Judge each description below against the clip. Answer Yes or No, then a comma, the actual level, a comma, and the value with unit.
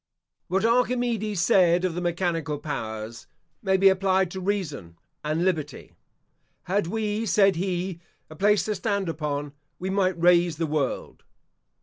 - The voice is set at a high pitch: No, medium, 180 Hz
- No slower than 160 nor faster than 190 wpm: No, average, 140 wpm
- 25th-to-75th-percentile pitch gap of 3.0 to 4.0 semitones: Yes, average, 3.5 semitones